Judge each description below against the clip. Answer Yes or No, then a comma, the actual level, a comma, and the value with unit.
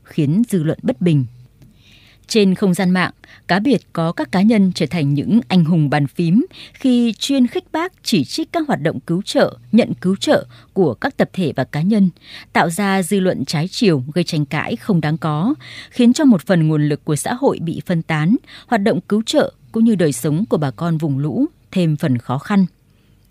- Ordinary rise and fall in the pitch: No, wide, 6.6 semitones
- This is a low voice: No, medium, 175 Hz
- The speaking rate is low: No, average, 215 wpm